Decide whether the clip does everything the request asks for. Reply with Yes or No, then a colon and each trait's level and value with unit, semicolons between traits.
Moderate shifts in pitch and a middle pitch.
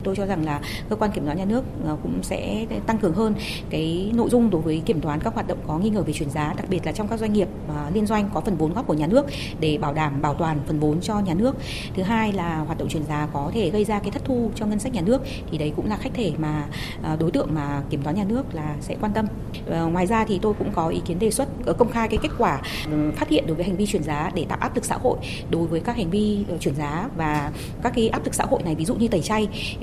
No: wide, 5.9 semitones; medium, 180 Hz